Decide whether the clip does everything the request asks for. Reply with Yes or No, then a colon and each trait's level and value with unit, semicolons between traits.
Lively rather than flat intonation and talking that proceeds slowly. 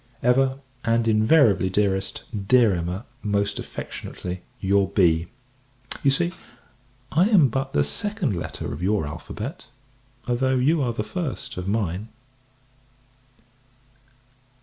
Yes: wide, 6.0 semitones; slow, 115 wpm